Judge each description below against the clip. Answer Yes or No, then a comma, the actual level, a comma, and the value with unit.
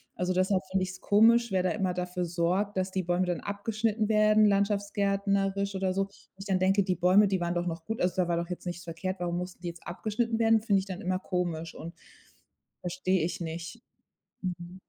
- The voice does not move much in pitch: Yes, narrow, 2.3 semitones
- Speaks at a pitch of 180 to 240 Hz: Yes, medium, 185 Hz